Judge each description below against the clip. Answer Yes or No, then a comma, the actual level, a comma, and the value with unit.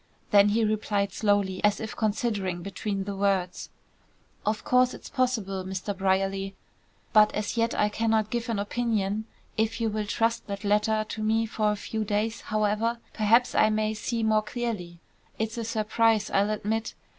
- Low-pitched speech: No, high, 215 Hz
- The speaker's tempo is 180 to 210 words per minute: No, average, 170 wpm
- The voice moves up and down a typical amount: No, narrow, 1.8 semitones